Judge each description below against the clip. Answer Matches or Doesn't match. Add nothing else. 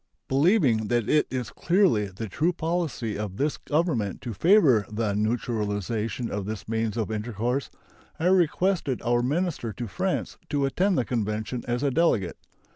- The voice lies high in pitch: Doesn't match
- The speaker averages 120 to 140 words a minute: Doesn't match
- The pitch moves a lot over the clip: Matches